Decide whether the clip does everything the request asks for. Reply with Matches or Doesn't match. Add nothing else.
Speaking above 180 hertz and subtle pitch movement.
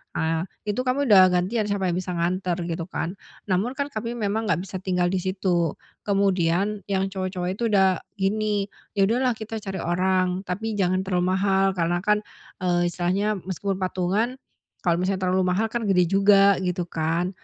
Matches